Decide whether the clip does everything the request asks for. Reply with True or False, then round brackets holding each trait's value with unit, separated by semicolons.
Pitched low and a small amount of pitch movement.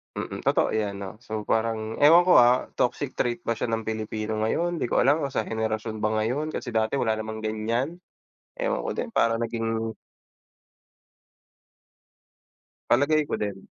False (115 Hz; 3.4 semitones)